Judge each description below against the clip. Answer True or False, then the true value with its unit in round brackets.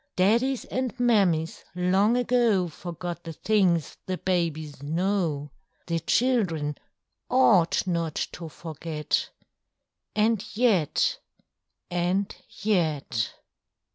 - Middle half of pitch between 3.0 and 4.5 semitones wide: False (5.0 semitones)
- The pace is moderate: False (85 wpm)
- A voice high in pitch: False (180 Hz)